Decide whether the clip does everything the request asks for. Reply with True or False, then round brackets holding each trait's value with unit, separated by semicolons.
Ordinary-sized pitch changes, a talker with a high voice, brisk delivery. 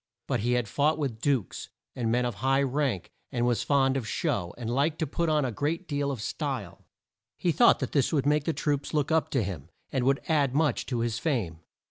False (3.7 semitones; 135 Hz; 225 wpm)